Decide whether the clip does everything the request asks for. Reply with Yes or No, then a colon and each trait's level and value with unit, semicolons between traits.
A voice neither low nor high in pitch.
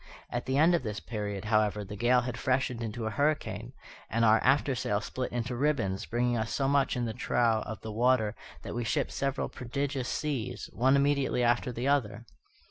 No: low, 120 Hz